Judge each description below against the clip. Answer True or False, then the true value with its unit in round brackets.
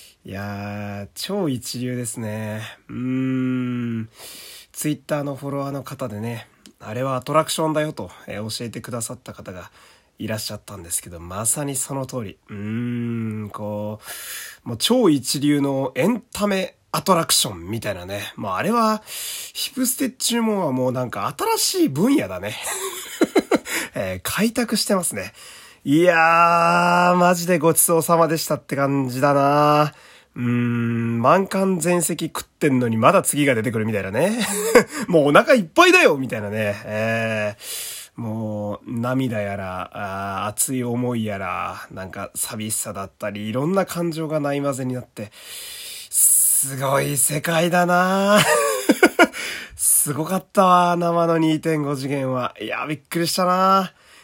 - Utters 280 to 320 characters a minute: True (285 characters per minute)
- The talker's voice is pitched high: False (135 Hz)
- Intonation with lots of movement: True (7.8 semitones)